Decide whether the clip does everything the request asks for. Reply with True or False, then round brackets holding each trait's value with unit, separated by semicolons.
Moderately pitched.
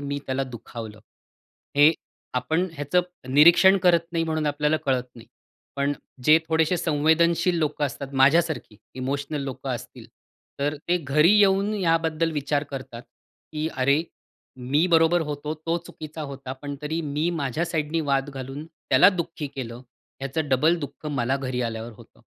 True (150 Hz)